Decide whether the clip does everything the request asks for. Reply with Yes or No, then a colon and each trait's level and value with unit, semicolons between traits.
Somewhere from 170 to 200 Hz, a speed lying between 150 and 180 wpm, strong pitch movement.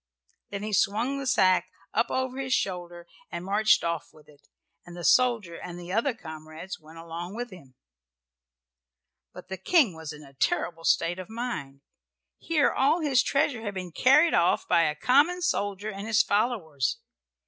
Yes: high, 190 Hz; average, 170 wpm; wide, 6.5 semitones